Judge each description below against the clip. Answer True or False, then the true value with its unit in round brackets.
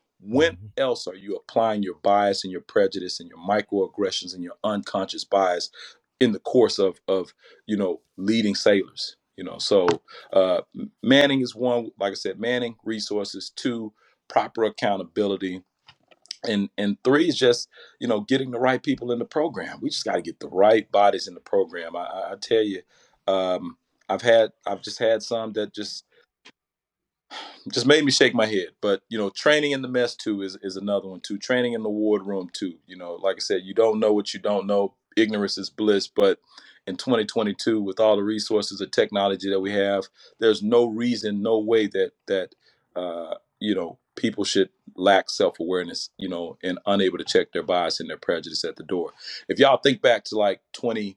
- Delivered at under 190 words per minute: False (195 wpm)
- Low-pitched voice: True (110 Hz)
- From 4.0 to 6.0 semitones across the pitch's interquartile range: True (4.9 semitones)